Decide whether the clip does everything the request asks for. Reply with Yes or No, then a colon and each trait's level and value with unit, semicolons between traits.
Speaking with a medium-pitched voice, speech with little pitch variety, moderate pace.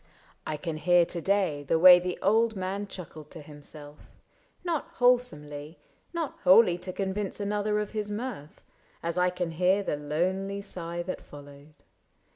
No: medium, 180 Hz; average, 4.7 semitones; average, 165 wpm